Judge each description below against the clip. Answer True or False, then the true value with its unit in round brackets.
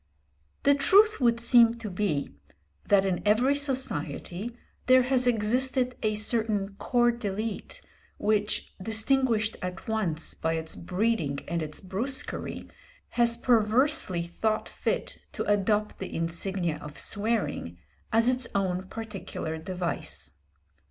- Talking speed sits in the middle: False (120 wpm)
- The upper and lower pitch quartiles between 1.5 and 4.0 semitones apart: False (4.8 semitones)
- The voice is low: False (215 Hz)